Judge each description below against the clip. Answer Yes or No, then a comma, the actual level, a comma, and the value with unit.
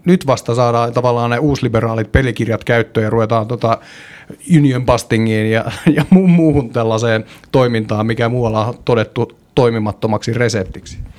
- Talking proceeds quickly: No, average, 125 wpm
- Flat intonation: Yes, narrow, 1.9 semitones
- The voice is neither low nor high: No, low, 115 Hz